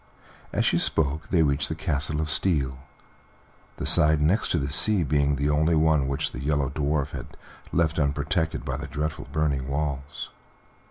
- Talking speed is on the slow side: No, average, 165 wpm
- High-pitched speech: No, very low, 75 Hz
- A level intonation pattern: Yes, narrow, 2.0 semitones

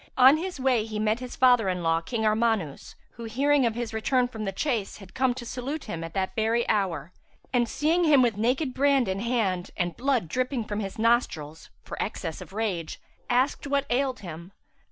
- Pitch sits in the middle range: No, high, 230 Hz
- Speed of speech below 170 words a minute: No, average, 200 wpm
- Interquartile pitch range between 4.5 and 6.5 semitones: Yes, average, 4.8 semitones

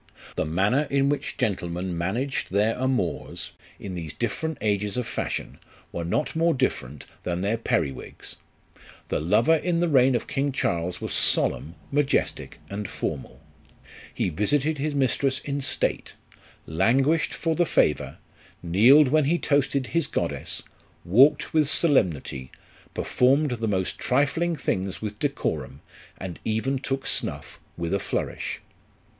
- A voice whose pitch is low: Yes, low, 125 Hz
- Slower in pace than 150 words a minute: Yes, average, 140 wpm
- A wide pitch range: Yes, wide, 7.4 semitones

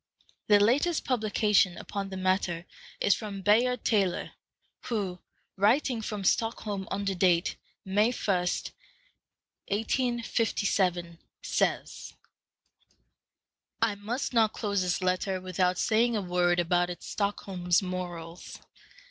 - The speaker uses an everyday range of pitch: Yes, average, 3.4 semitones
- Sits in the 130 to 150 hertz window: No, high, 200 Hz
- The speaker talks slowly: Yes, slow, 105 wpm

